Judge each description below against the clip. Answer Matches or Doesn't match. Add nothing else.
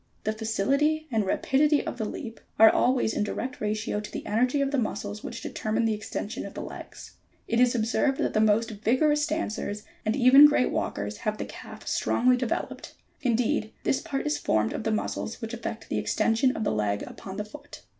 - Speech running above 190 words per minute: Matches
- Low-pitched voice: Doesn't match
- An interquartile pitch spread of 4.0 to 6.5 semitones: Doesn't match